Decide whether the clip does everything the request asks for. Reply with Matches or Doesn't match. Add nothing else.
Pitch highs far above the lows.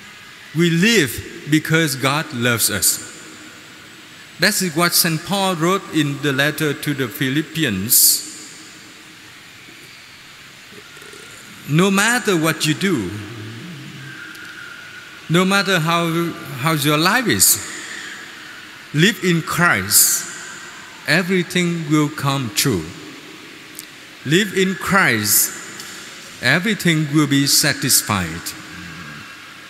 Doesn't match